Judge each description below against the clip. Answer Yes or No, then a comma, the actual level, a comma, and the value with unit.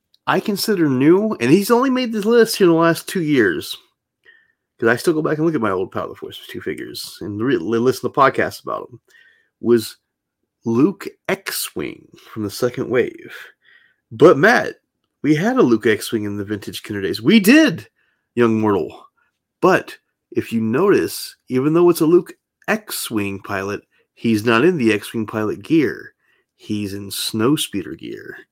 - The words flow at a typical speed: Yes, average, 185 wpm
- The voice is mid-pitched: Yes, medium, 155 Hz